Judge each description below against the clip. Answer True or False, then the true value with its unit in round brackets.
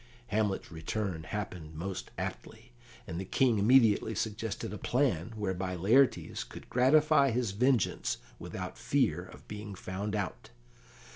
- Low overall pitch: True (105 Hz)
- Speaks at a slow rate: True (130 wpm)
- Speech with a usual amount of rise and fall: True (4.2 semitones)